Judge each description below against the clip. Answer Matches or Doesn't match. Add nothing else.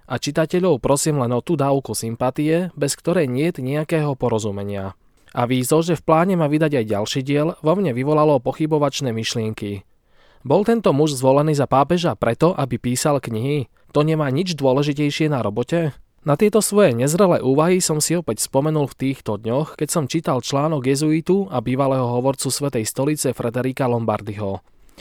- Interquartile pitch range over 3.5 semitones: Matches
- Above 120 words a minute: Matches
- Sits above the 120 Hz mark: Matches